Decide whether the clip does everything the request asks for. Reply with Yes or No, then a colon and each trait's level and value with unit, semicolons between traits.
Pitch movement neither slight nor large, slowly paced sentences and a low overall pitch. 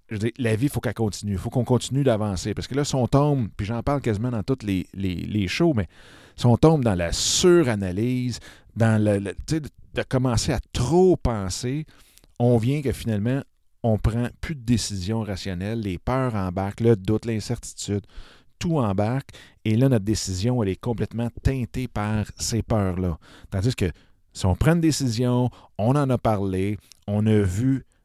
No: average, 4.0 semitones; average, 190 wpm; low, 115 Hz